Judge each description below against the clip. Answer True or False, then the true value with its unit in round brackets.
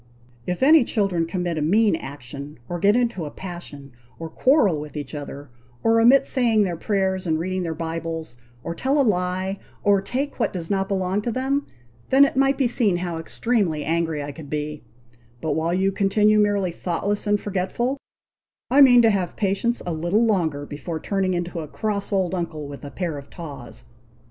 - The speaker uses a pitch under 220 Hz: True (185 Hz)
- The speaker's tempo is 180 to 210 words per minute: True (190 wpm)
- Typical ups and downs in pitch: True (4.7 semitones)